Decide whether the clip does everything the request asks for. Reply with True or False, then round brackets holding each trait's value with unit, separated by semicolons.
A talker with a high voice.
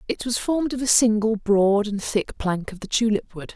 True (215 Hz)